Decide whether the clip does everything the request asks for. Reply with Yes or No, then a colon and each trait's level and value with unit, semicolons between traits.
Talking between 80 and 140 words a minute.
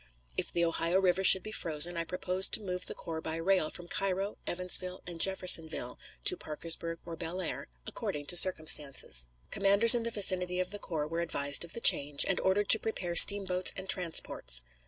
No: average, 185 wpm